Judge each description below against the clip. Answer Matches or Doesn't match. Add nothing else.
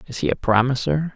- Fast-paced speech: Matches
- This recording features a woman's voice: Doesn't match